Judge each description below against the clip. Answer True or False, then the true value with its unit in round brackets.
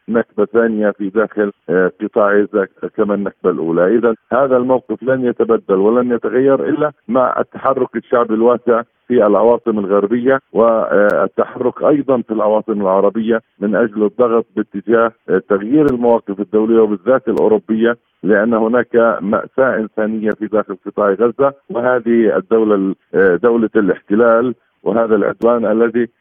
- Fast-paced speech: False (120 wpm)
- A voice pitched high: False (115 Hz)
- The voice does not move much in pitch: True (2.2 semitones)